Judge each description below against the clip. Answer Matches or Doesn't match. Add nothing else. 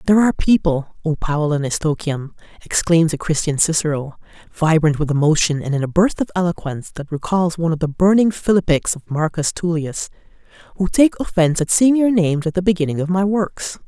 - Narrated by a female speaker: Matches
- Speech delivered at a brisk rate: Doesn't match